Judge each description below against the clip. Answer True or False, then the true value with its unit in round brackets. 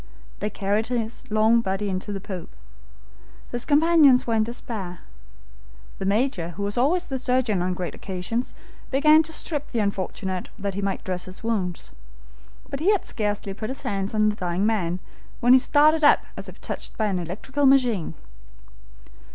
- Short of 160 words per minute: False (175 wpm)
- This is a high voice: True (215 Hz)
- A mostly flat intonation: False (5.1 semitones)